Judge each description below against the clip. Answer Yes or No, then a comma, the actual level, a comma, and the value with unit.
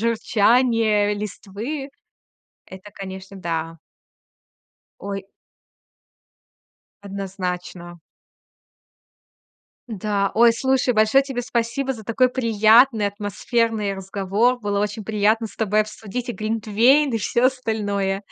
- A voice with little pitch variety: No, average, 3.0 semitones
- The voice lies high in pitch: Yes, high, 215 Hz